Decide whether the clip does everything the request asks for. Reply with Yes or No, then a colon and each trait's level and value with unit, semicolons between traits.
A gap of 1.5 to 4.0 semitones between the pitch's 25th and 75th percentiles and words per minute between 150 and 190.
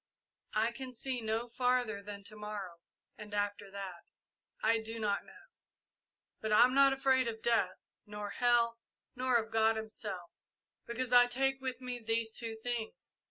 Yes: average, 2.8 semitones; average, 160 wpm